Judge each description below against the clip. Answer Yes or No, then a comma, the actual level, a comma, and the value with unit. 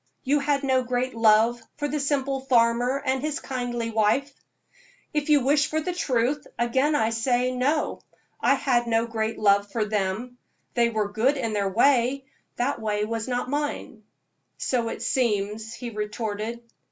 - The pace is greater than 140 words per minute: Yes, average, 165 wpm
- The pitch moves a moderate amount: Yes, average, 3.6 semitones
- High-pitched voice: Yes, high, 245 Hz